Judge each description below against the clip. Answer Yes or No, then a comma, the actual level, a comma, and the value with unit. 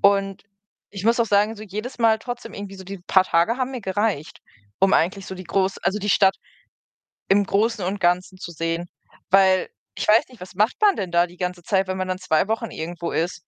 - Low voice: No, high, 195 Hz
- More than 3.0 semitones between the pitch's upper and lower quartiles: No, narrow, 2.6 semitones